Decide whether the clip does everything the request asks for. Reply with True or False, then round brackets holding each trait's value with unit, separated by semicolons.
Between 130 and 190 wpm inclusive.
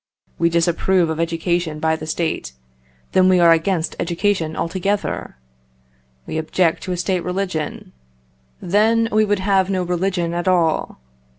True (140 wpm)